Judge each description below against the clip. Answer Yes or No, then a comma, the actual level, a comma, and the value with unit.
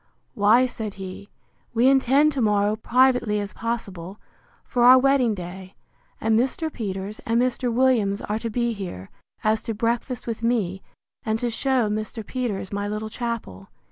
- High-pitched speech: Yes, high, 225 Hz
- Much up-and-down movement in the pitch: No, average, 3.3 semitones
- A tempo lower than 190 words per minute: Yes, average, 160 wpm